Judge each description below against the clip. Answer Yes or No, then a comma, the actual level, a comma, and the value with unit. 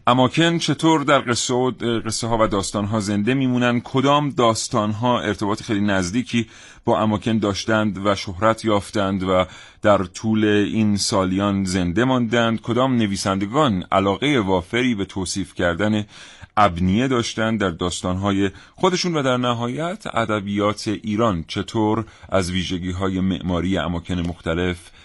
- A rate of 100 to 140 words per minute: Yes, average, 130 wpm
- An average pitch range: Yes, average, 3.7 semitones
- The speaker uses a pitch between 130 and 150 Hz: No, low, 105 Hz